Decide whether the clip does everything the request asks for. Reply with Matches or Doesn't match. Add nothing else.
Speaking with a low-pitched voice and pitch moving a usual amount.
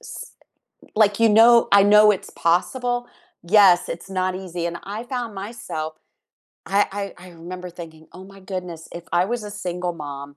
Doesn't match